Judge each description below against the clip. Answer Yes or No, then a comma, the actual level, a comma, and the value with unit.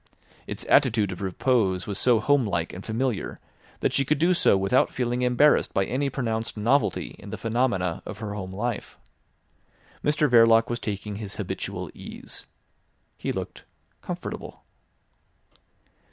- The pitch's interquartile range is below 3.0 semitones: No, average, 4.3 semitones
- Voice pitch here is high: No, low, 115 Hz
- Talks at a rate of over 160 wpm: No, average, 145 wpm